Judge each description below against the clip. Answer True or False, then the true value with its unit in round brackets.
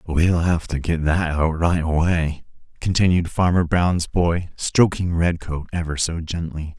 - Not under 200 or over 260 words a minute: False (150 wpm)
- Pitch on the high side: False (85 Hz)